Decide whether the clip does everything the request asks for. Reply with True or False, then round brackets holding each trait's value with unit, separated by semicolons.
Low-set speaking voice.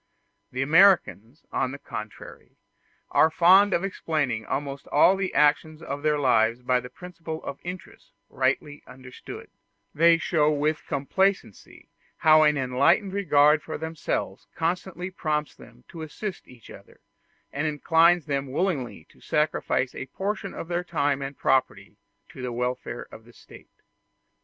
False (150 Hz)